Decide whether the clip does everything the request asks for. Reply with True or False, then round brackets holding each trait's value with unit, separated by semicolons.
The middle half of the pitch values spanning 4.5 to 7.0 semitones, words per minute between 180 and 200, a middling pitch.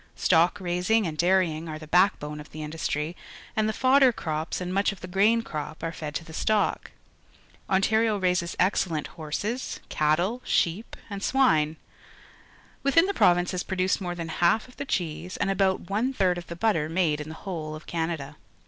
False (4.1 semitones; 185 wpm; 180 Hz)